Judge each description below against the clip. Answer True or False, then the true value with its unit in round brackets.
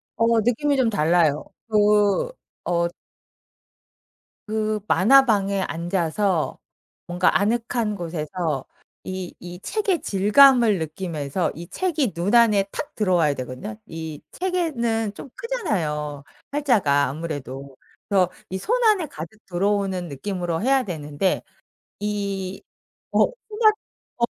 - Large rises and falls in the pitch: True (5.8 semitones)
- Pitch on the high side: True (195 Hz)